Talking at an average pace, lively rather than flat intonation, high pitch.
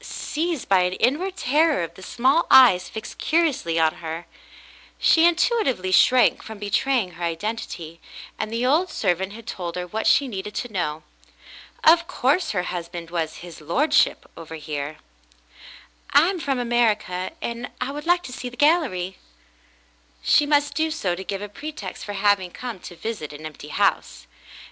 Yes: average, 170 wpm; wide, 8.3 semitones; high, 215 Hz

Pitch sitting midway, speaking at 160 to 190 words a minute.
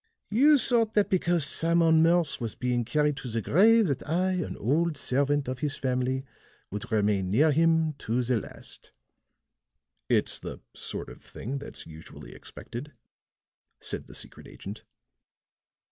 No: medium, 145 Hz; average, 145 wpm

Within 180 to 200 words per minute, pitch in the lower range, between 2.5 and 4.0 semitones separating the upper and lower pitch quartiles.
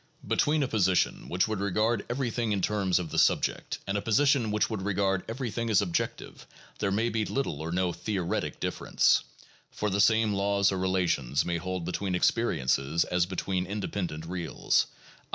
Yes: average, 185 wpm; low, 100 Hz; average, 3.3 semitones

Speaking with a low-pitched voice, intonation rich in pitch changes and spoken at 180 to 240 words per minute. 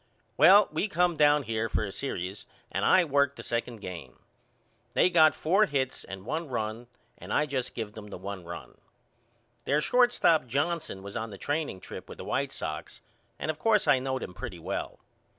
Yes: low, 130 Hz; wide, 7.1 semitones; average, 190 wpm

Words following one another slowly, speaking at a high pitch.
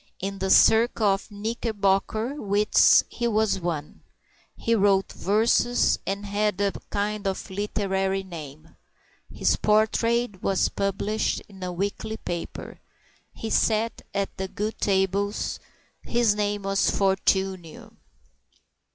Yes: slow, 115 wpm; high, 200 Hz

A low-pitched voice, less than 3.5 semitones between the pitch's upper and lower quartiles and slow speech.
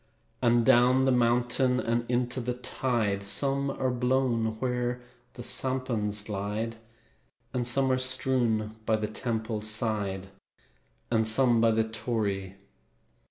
Yes: low, 120 Hz; narrow, 2.5 semitones; slow, 125 wpm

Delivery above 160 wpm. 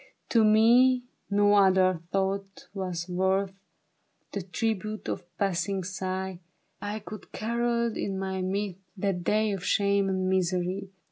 No: average, 140 wpm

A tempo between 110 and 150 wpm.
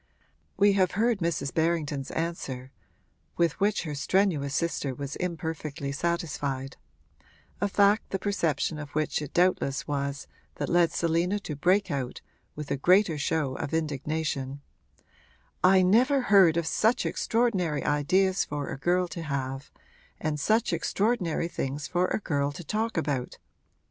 Yes: average, 145 wpm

